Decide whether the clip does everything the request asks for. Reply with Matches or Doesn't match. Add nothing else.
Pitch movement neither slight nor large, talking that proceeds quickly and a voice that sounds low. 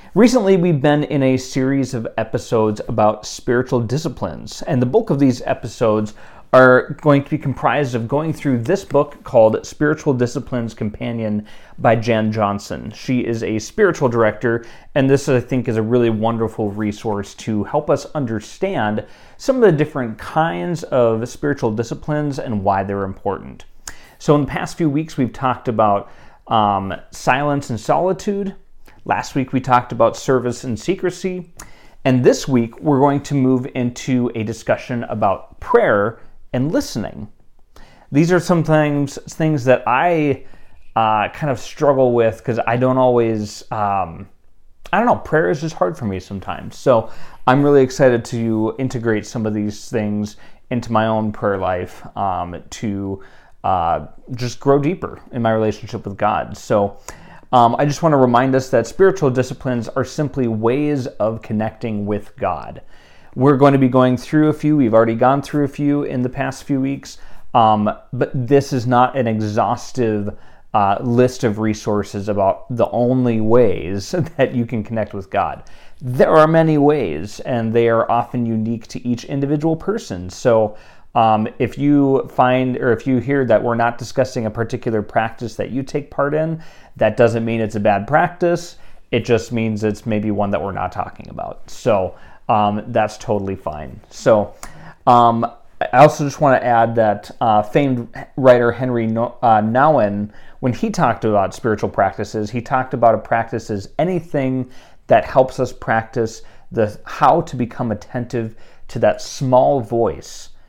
Doesn't match